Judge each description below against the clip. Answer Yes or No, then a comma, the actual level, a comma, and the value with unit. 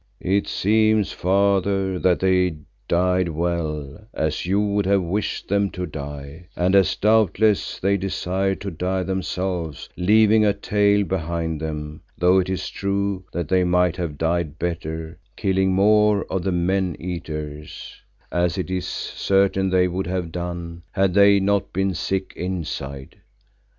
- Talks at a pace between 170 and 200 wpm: No, average, 145 wpm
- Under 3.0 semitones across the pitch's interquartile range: Yes, narrow, 2.5 semitones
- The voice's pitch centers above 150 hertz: No, very low, 90 Hz